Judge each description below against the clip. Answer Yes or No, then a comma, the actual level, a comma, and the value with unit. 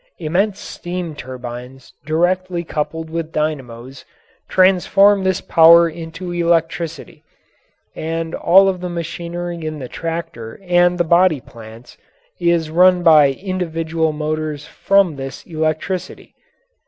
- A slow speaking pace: Yes, slow, 115 wpm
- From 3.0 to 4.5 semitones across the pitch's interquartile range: No, narrow, 2.5 semitones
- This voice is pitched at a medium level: Yes, medium, 165 Hz